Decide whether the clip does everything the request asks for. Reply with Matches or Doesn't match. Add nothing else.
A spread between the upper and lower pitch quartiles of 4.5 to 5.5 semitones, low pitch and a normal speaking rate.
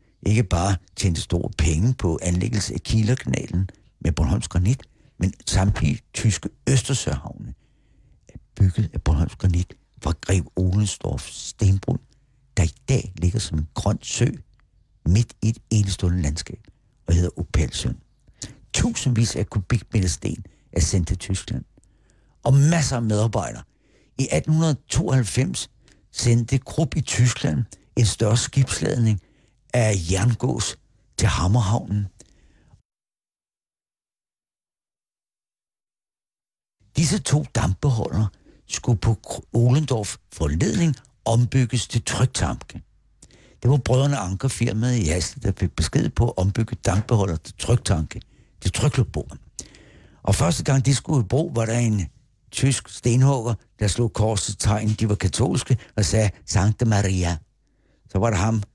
Doesn't match